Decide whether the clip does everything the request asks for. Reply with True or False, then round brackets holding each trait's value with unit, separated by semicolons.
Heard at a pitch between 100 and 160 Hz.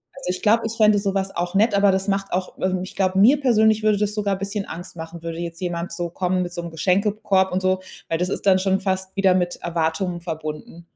False (190 Hz)